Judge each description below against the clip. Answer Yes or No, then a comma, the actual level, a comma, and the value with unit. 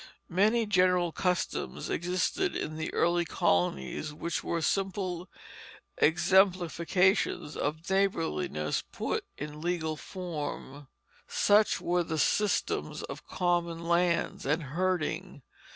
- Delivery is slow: Yes, slow, 105 wpm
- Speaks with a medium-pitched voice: Yes, medium, 175 Hz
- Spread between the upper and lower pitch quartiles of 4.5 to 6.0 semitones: No, average, 3.0 semitones